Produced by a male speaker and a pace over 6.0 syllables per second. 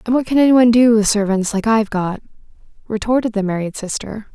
No: female; 6.5 syllables/s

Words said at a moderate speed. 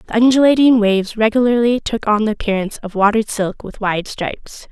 Yes: average, 180 wpm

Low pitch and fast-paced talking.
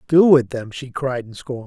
Yes: low, 130 Hz; fast, 250 wpm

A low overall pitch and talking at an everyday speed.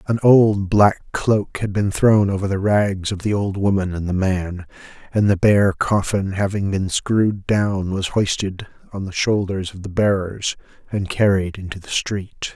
Yes: low, 100 Hz; average, 180 wpm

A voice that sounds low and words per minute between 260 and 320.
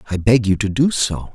Yes: low, 110 Hz; fast, 265 wpm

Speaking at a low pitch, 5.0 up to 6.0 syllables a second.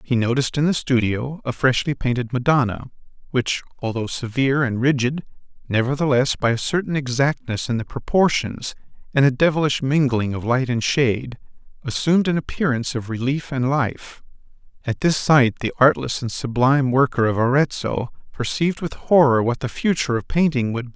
Yes: low, 130 Hz; 5.4 syllables/s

